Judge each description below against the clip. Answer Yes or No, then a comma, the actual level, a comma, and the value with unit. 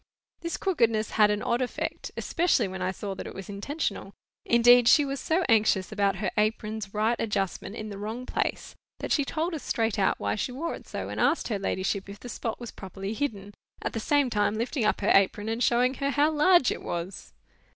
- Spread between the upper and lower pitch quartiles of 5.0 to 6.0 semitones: No, average, 4.4 semitones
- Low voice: No, high, 220 Hz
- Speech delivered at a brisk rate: Yes, fast, 215 wpm